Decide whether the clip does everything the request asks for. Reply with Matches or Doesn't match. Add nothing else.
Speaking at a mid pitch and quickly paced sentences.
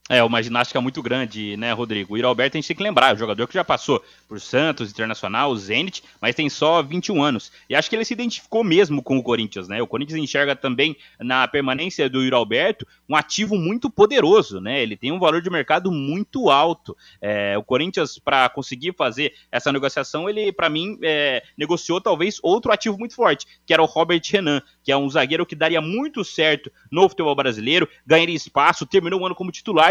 Matches